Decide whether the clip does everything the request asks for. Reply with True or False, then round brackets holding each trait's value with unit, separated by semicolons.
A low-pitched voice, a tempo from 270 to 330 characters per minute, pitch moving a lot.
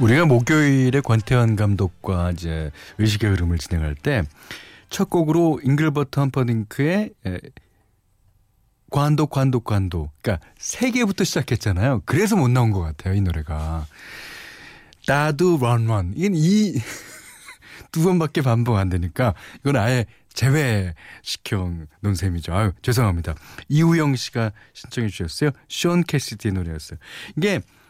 True (115 Hz; 285 characters per minute; 7.3 semitones)